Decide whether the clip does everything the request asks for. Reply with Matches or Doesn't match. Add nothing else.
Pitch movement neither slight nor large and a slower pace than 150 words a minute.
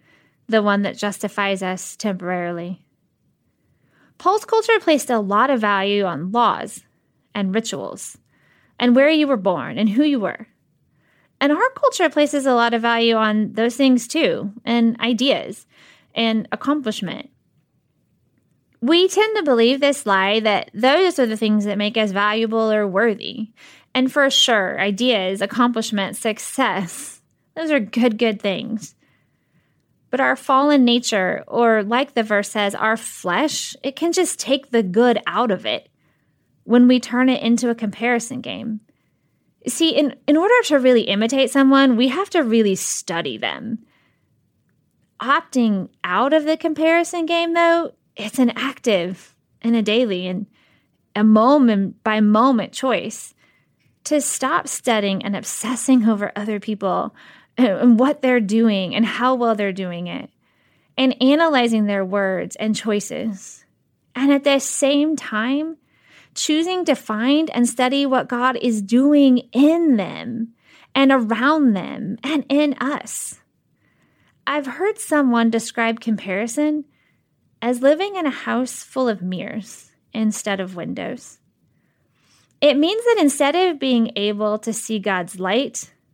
Matches